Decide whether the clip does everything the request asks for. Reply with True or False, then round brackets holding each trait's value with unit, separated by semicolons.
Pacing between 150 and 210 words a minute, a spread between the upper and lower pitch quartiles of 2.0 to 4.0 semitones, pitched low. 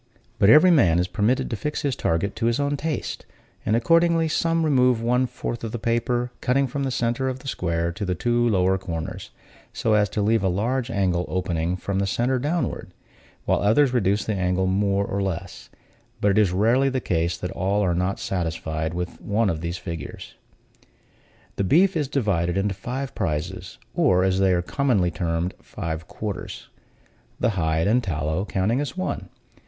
False (185 wpm; 5.6 semitones; 100 Hz)